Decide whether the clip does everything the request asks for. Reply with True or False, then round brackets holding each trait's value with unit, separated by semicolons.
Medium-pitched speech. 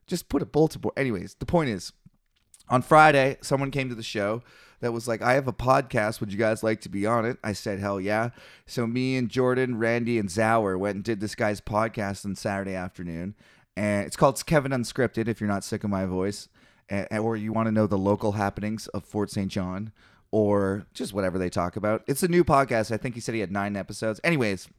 False (110 Hz)